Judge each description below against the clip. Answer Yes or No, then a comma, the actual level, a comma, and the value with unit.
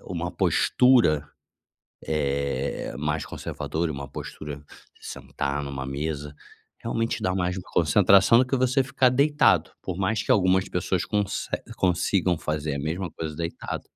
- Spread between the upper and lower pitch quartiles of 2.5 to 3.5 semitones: No, average, 5.0 semitones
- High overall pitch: No, very low, 85 Hz